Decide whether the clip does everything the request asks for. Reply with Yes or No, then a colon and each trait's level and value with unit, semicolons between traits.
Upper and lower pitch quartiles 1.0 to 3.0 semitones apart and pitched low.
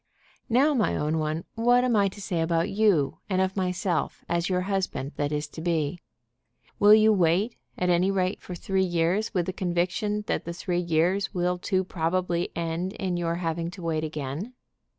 No: average, 2.7 semitones; medium, 180 Hz